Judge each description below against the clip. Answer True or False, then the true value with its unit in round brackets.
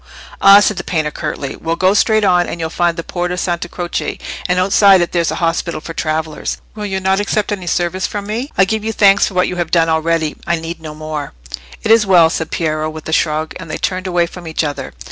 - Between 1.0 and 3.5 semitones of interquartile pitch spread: True (3.0 semitones)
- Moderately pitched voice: True (175 Hz)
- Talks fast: True (240 wpm)